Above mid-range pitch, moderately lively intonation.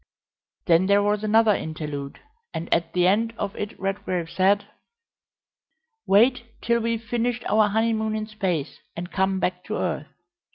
Yes: high, 200 Hz; average, 3.5 semitones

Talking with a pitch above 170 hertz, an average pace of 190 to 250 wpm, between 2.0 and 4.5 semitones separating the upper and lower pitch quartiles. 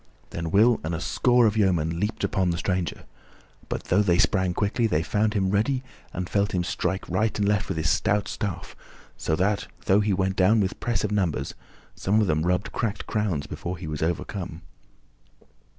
No: very low, 95 Hz; average, 195 wpm; average, 3.2 semitones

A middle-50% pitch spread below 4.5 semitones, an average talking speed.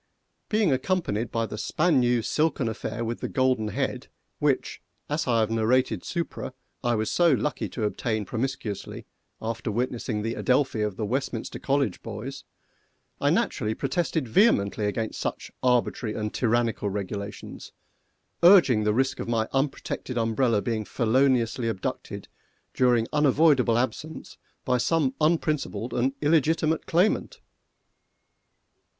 No: average, 4.0 semitones; slow, 130 wpm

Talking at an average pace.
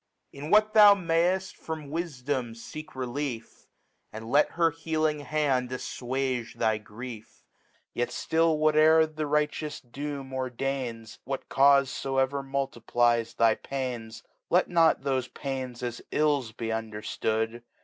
No: slow, 125 wpm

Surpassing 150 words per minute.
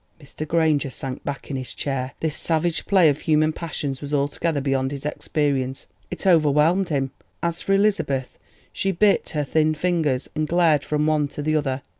Yes: average, 175 wpm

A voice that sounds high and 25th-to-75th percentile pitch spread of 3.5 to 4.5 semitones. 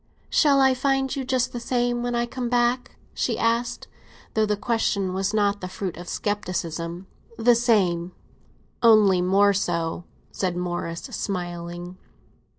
No: high, 205 Hz; average, 5.2 semitones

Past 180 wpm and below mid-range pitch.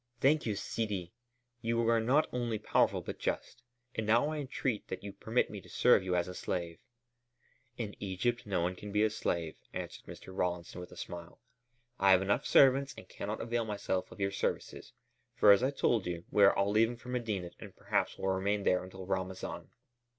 Yes: average, 200 wpm; low, 105 Hz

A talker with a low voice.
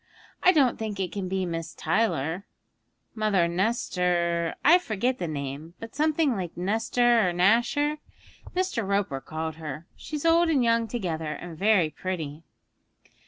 No: high, 195 Hz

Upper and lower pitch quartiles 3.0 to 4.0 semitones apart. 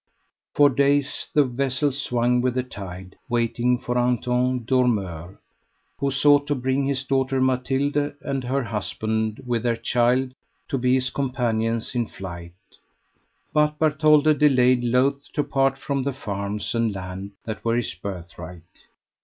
Yes: average, 3.3 semitones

